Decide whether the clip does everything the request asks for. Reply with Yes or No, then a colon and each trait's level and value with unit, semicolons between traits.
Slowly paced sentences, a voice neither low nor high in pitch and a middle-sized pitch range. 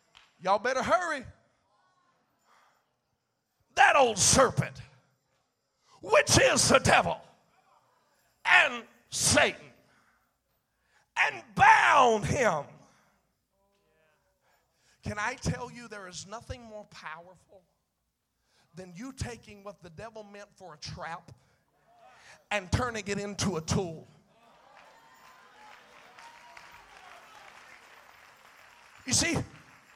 No: slow, 85 wpm; high, 205 Hz; average, 3.8 semitones